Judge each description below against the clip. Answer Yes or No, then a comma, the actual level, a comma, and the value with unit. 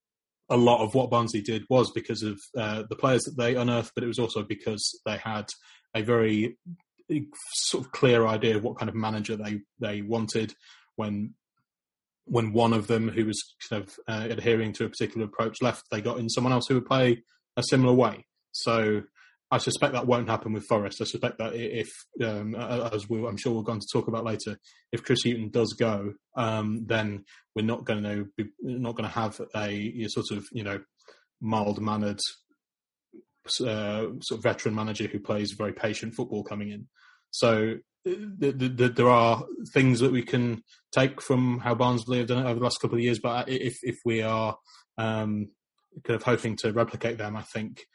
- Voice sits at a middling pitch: No, low, 115 Hz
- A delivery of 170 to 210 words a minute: Yes, average, 200 wpm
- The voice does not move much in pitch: Yes, narrow, 2.0 semitones